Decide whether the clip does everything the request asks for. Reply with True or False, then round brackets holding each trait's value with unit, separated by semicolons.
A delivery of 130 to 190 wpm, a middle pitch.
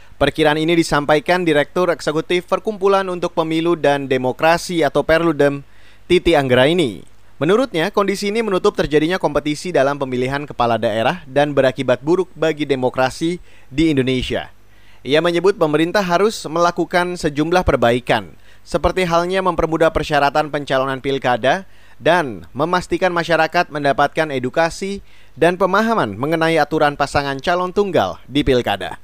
False (120 wpm; 155 Hz)